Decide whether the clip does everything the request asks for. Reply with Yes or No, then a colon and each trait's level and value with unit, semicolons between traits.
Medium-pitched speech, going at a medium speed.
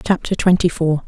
Yes: medium, 170 Hz; average, 165 wpm